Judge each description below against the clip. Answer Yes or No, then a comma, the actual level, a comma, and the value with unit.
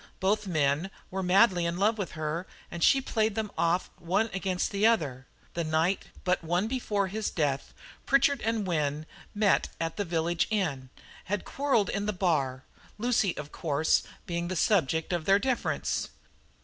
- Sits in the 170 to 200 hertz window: Yes, medium, 185 Hz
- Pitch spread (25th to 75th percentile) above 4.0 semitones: Yes, average, 4.5 semitones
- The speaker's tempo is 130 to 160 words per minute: No, average, 170 wpm